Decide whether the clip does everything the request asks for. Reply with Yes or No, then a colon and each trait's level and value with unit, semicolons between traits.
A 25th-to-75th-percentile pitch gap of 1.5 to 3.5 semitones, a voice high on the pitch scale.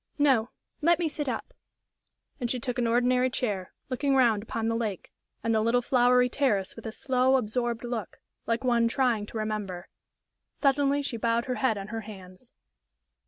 Yes: average, 2.7 semitones; high, 240 Hz